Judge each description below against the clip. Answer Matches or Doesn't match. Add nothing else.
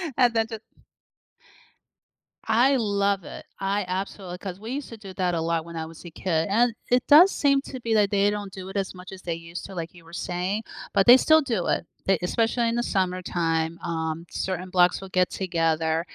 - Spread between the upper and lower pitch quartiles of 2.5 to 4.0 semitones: Doesn't match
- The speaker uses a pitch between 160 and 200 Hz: Matches